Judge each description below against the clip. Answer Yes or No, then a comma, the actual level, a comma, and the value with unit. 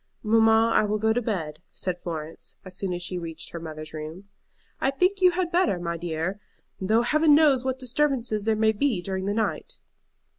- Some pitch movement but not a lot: No, wide, 6.5 semitones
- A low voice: No, high, 215 Hz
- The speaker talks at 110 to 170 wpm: No, average, 195 wpm